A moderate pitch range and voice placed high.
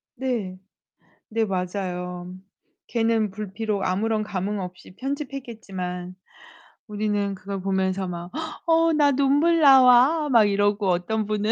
Yes: average, 4.7 semitones; high, 210 Hz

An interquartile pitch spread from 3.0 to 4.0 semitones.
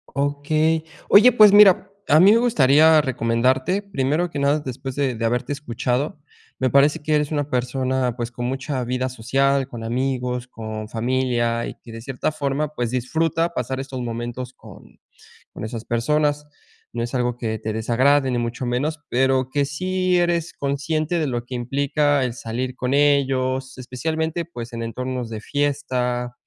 Yes: average, 3.3 semitones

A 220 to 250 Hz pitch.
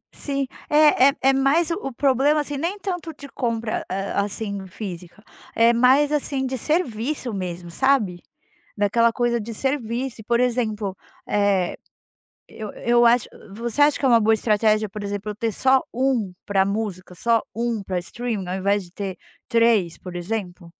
Yes: high, 230 Hz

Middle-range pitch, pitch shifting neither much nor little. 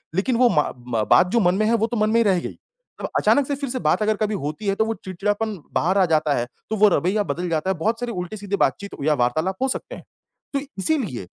No: high, 200 Hz; average, 4.6 semitones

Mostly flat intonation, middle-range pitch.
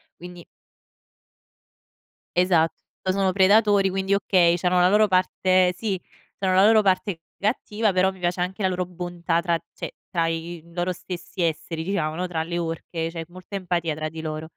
Yes: narrow, 2.1 semitones; medium, 180 Hz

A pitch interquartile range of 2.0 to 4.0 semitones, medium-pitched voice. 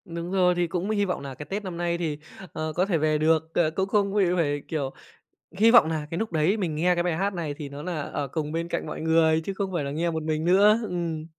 Yes: average, 3.1 semitones; medium, 170 Hz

